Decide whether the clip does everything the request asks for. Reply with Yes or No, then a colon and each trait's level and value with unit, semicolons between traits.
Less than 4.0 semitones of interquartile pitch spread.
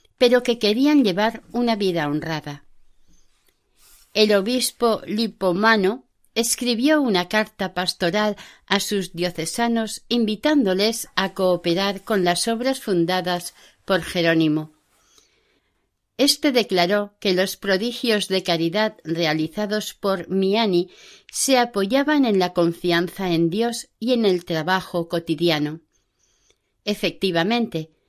No: average, 4.7 semitones